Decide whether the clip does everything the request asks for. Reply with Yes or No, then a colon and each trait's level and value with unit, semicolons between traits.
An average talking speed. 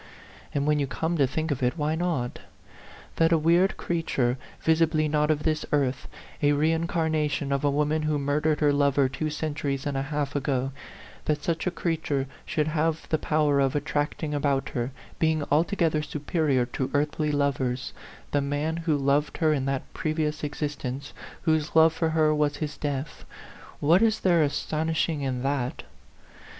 Yes: average, 170 wpm